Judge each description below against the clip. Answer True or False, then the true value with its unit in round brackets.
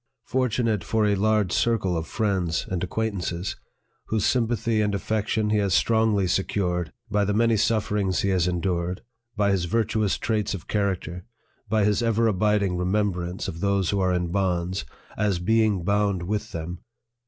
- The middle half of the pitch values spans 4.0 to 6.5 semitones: False (3.1 semitones)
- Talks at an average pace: True (165 wpm)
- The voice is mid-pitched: False (100 Hz)